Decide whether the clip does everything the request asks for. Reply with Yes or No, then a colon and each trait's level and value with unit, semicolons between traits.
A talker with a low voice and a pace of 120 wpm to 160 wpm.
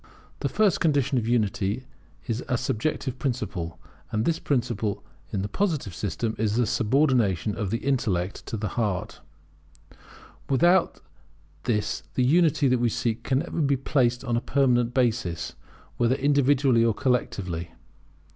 Yes: low, 120 Hz; average, 145 wpm